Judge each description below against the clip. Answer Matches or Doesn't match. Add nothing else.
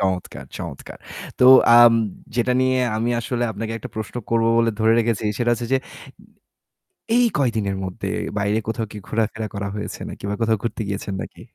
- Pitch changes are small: Matches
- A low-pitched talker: Matches